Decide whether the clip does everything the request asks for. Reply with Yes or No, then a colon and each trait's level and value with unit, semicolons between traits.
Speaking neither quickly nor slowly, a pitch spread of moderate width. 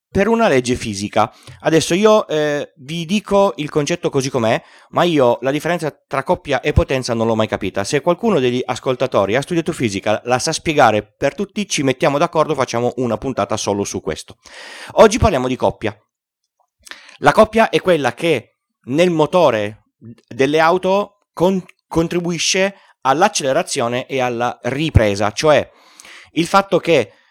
No: average, 150 wpm; wide, 6.0 semitones